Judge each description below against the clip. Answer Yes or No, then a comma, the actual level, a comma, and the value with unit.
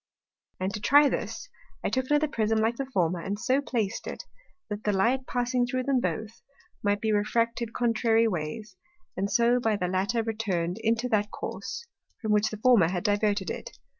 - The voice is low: No, high, 220 Hz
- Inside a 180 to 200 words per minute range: Yes, average, 185 wpm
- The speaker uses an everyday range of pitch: Yes, average, 3.1 semitones